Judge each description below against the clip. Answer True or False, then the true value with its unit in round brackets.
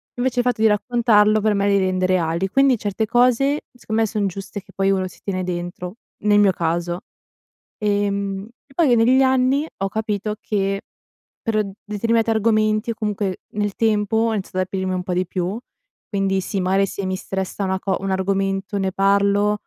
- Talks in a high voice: True (200 Hz)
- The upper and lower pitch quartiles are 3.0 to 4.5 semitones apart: False (2.5 semitones)